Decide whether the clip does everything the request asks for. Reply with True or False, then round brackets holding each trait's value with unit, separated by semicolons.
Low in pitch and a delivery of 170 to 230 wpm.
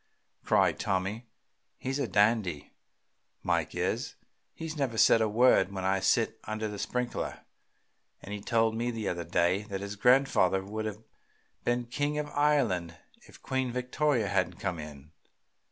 False (110 Hz; 155 wpm)